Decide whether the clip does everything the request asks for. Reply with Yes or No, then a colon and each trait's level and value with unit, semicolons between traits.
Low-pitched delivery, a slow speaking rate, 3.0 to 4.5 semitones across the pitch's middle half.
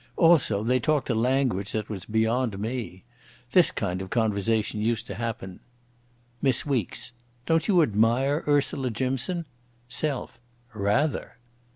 Yes: low, 120 Hz; slow, 125 wpm; average, 3.7 semitones